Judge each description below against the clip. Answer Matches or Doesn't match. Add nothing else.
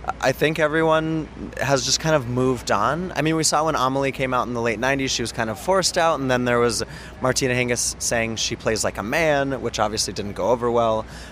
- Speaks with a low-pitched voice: Matches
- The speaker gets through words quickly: Matches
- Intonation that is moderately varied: Matches